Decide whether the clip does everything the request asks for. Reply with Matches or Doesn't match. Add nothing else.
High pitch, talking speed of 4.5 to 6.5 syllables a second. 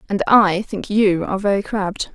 Matches